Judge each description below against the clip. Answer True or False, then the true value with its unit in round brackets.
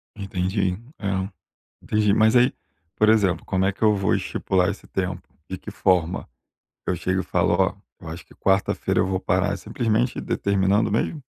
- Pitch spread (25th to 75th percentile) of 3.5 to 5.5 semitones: False (2.5 semitones)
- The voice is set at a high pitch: False (95 Hz)